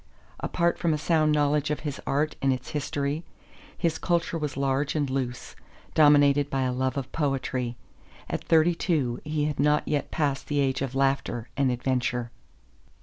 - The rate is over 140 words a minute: Yes, average, 170 wpm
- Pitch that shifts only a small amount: Yes, narrow, 2.3 semitones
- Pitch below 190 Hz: Yes, medium, 140 Hz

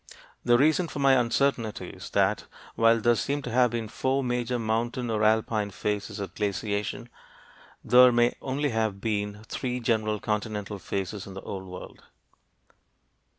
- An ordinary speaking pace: Yes, average, 150 wpm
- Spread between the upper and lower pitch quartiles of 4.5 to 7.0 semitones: No, average, 2.9 semitones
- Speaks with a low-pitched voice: Yes, low, 115 Hz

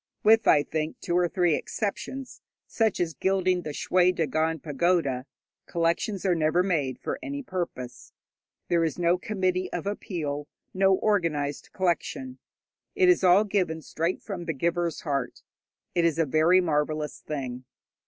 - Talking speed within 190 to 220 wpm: No, average, 150 wpm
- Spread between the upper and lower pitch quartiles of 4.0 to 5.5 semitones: No, average, 3.4 semitones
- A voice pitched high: No, medium, 175 Hz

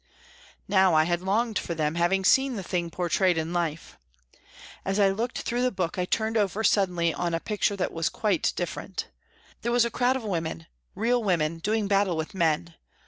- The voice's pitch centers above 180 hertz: Yes, high, 190 Hz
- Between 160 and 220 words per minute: Yes, average, 195 wpm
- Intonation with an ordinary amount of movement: Yes, average, 4.2 semitones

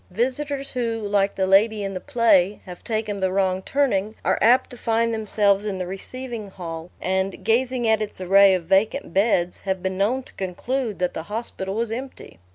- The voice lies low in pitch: No, high, 205 Hz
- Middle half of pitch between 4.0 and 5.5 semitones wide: No, average, 3.5 semitones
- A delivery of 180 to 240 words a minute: Yes, average, 190 wpm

